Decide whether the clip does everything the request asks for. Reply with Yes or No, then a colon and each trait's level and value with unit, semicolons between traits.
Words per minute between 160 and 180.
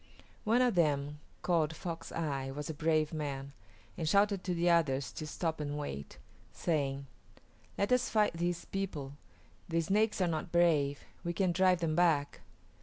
Yes: average, 165 wpm